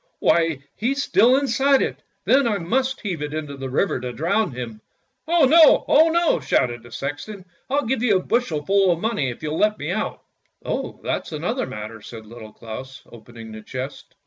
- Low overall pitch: No, medium, 165 Hz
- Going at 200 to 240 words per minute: Yes, fast, 205 wpm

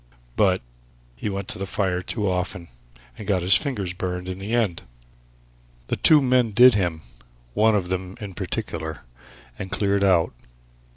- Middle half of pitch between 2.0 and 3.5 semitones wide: Yes, narrow, 2.6 semitones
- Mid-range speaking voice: No, very low, 95 Hz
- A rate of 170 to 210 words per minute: No, average, 160 wpm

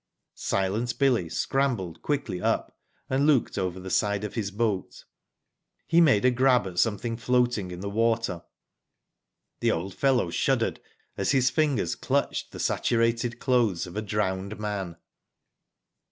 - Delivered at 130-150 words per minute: Yes, average, 140 wpm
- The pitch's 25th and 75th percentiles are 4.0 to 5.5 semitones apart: Yes, average, 4.6 semitones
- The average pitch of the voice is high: No, low, 110 Hz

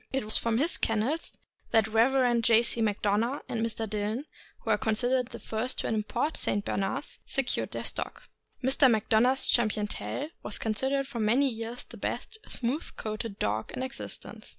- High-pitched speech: Yes, high, 230 Hz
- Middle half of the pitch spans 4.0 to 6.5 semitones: No, average, 3.3 semitones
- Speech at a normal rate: Yes, average, 175 wpm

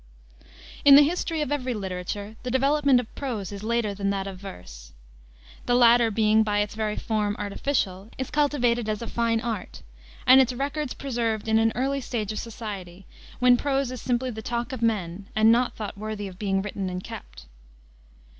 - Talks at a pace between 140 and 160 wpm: No, average, 185 wpm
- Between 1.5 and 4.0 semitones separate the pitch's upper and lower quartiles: Yes, average, 3.7 semitones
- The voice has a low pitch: No, high, 225 Hz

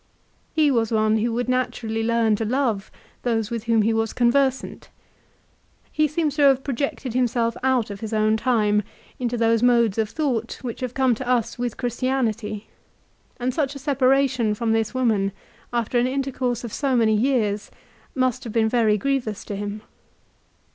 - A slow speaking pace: No, average, 170 wpm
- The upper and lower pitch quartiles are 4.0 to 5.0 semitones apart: No, average, 2.7 semitones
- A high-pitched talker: Yes, high, 235 Hz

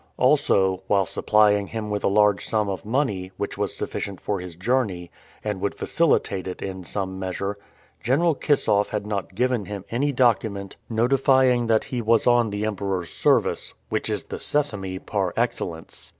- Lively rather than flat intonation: No, average, 3.8 semitones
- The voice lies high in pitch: No, low, 105 Hz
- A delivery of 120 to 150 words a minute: No, average, 165 wpm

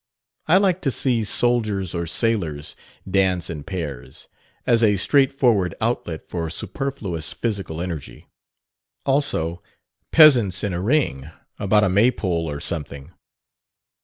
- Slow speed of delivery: Yes, slow, 120 wpm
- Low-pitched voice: Yes, very low, 95 Hz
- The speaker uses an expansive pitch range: Yes, wide, 6.4 semitones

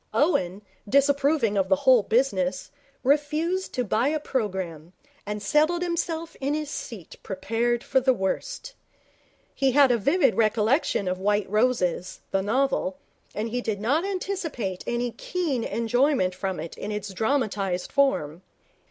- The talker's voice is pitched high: Yes, high, 235 Hz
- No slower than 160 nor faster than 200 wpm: No, average, 145 wpm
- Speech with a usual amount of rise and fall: No, wide, 6.5 semitones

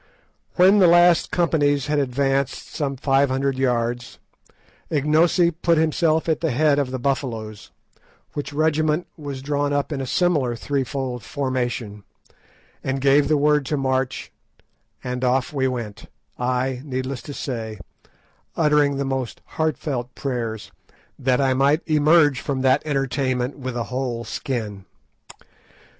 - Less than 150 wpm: Yes, average, 140 wpm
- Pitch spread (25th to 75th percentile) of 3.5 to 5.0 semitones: No, average, 2.9 semitones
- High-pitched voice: No, low, 135 Hz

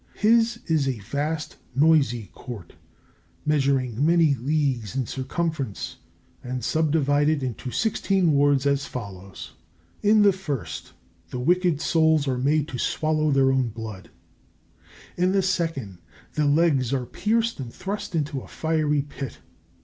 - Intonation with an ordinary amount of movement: Yes, average, 4.0 semitones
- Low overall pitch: No, medium, 145 Hz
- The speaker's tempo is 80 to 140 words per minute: Yes, slow, 135 wpm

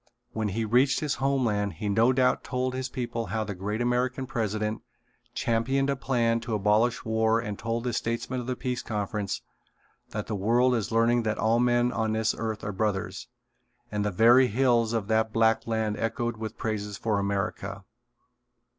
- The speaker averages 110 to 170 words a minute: No, average, 180 wpm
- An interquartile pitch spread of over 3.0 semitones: No, narrow, 2.4 semitones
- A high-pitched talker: No, low, 115 Hz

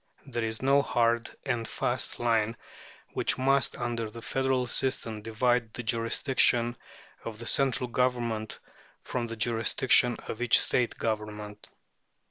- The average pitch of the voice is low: Yes, low, 120 Hz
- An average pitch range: No, narrow, 1.9 semitones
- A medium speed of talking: No, slow, 130 wpm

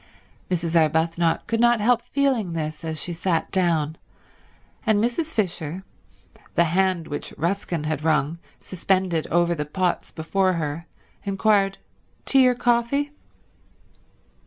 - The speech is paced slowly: Yes, slow, 125 wpm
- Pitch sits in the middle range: Yes, medium, 175 Hz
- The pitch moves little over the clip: No, average, 4.8 semitones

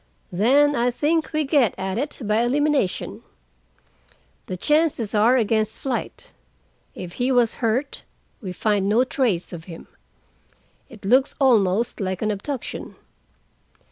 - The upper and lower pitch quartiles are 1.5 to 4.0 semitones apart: No, average, 5.2 semitones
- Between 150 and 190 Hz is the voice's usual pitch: No, high, 235 Hz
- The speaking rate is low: Yes, slow, 130 wpm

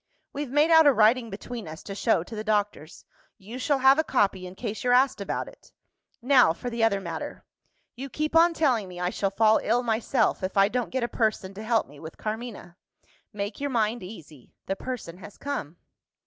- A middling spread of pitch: Yes, average, 4.5 semitones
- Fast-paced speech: Yes, fast, 210 wpm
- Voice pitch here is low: No, high, 220 Hz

